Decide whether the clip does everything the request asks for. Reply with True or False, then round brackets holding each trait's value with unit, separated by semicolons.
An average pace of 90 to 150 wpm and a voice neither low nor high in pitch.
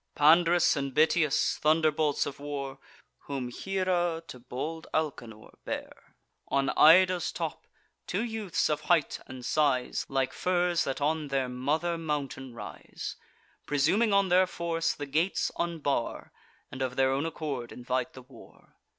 True (140 wpm; 150 Hz)